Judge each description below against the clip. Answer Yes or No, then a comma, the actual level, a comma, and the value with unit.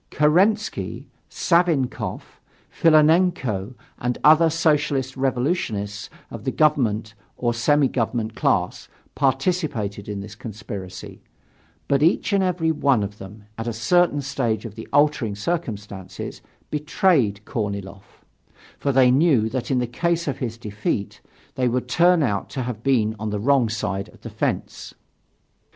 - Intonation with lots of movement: Yes, wide, 6.0 semitones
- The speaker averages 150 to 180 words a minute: No, slow, 135 wpm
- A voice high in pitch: No, low, 125 Hz